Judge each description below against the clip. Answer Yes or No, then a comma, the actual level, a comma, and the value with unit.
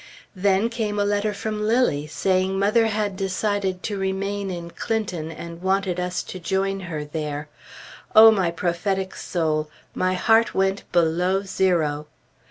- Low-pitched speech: No, high, 190 Hz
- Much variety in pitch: No, average, 2.9 semitones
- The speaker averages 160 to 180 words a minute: No, average, 145 wpm